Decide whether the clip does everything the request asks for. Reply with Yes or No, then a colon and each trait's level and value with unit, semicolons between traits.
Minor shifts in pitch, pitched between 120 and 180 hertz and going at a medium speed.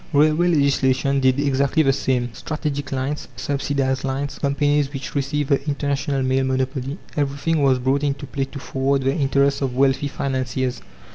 Yes: narrow, 1.3 semitones; medium, 140 Hz; average, 155 wpm